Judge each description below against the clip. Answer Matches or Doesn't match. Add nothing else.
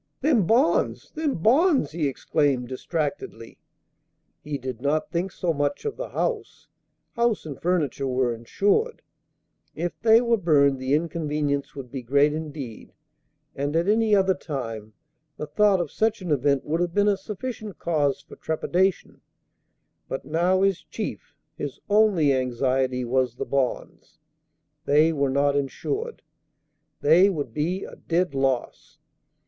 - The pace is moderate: Matches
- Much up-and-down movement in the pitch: Matches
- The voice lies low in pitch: Doesn't match